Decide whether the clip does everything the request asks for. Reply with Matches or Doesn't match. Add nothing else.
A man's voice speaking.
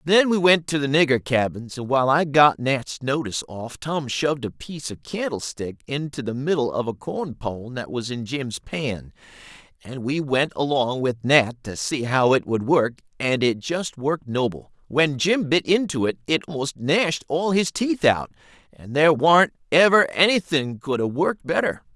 Matches